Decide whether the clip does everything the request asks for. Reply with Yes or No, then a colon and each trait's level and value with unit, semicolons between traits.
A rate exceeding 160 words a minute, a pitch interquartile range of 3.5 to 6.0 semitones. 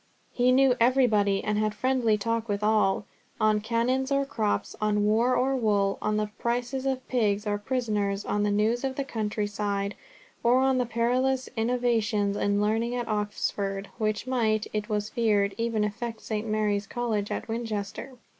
No: average, 170 wpm; average, 2.8 semitones